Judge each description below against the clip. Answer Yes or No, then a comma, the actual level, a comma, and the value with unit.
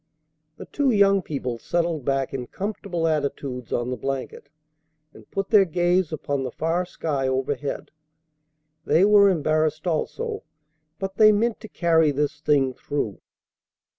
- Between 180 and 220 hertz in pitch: No, medium, 155 Hz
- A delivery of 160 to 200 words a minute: No, average, 140 wpm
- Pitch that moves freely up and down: Yes, wide, 5.9 semitones